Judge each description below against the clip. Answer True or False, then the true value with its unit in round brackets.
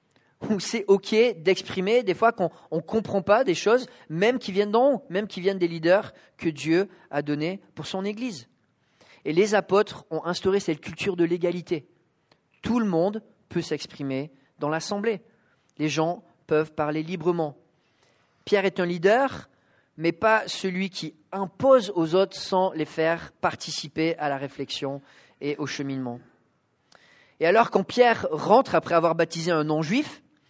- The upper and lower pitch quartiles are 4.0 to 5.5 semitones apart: True (4.5 semitones)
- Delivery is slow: False (160 wpm)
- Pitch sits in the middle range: True (175 Hz)